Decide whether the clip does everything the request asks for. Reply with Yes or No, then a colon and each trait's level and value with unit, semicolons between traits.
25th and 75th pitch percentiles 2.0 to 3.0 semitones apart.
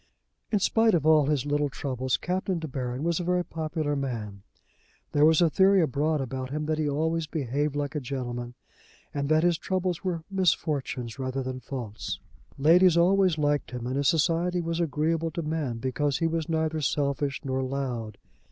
No: average, 3.9 semitones